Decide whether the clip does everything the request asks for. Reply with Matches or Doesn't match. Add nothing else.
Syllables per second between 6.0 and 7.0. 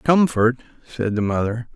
Doesn't match